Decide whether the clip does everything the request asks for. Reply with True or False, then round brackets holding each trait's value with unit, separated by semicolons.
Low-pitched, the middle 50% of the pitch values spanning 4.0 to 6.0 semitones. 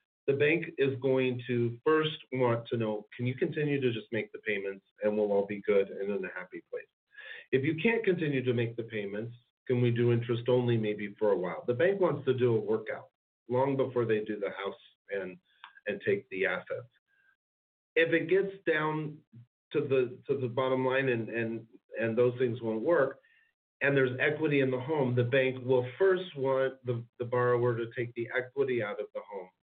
True (130 Hz; 4.9 semitones)